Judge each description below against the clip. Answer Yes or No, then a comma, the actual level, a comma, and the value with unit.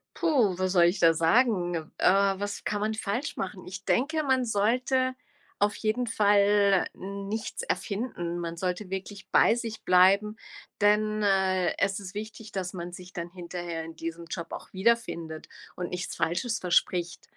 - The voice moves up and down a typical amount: Yes, average, 3.2 semitones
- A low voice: No, high, 195 Hz